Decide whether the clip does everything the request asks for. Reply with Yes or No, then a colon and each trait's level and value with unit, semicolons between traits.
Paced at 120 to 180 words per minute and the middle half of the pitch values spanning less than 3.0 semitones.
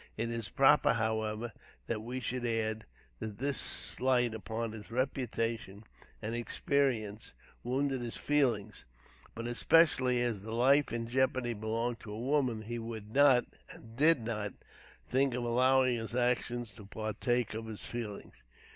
Yes: average, 145 wpm; narrow, 2.5 semitones